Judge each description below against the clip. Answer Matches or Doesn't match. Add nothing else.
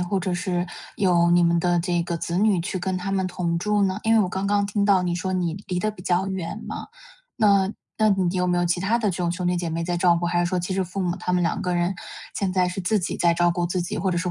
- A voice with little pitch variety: Matches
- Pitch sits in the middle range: Matches